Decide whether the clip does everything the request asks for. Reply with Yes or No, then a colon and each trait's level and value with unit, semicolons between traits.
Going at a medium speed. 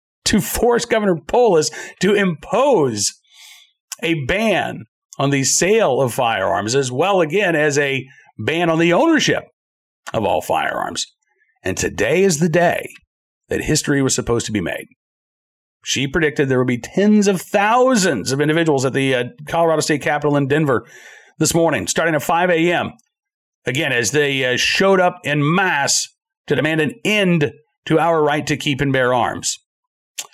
Yes: average, 160 wpm